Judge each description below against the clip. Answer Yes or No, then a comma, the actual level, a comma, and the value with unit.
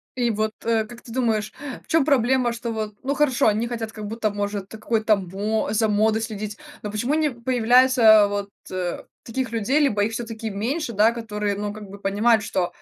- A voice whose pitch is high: Yes, high, 220 Hz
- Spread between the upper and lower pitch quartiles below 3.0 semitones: Yes, narrow, 2.4 semitones